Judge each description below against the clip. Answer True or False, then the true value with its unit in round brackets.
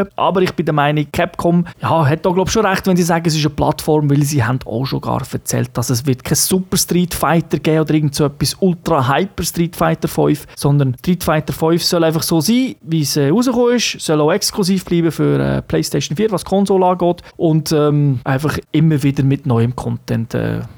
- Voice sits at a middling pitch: True (160 Hz)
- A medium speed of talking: False (220 wpm)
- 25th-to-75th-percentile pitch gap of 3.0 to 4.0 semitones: True (3.6 semitones)